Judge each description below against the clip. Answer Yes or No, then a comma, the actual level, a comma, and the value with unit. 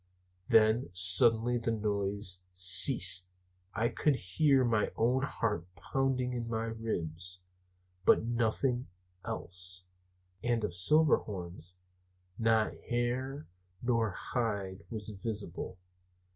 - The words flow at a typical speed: No, slow, 100 wpm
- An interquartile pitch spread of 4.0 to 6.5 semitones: Yes, average, 4.4 semitones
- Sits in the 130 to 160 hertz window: No, low, 110 Hz